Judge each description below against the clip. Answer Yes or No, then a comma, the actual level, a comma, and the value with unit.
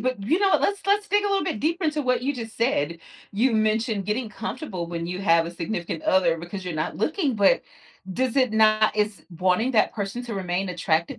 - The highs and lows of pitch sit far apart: Yes, wide, 6.0 semitones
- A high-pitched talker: Yes, high, 215 Hz